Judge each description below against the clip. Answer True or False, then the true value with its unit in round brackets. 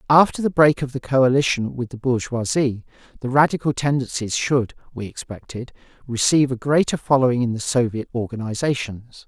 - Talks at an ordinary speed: True (150 wpm)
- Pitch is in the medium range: False (130 Hz)